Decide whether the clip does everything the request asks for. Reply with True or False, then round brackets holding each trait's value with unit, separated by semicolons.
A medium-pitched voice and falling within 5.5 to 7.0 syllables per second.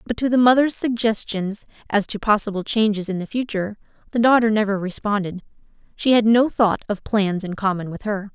False (210 Hz; 5.6 syllables/s)